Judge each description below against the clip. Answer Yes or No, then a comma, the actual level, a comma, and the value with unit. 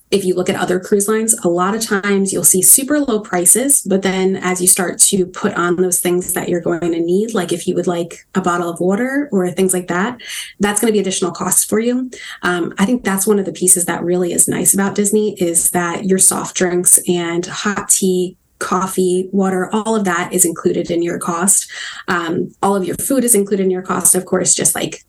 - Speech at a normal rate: No, fast, 235 wpm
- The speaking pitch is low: No, medium, 185 Hz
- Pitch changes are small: Yes, narrow, 2.2 semitones